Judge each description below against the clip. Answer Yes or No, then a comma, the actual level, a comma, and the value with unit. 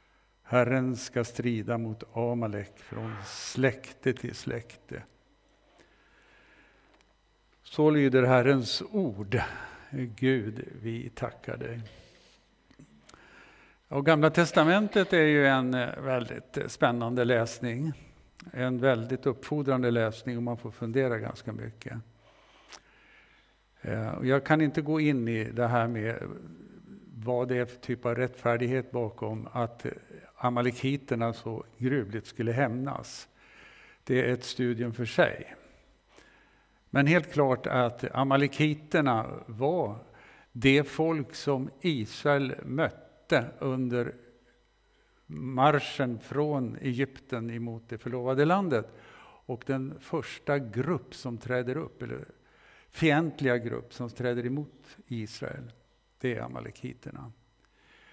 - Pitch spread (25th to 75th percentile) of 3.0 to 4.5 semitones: No, narrow, 2.6 semitones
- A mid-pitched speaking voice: No, low, 125 Hz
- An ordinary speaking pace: No, slow, 105 wpm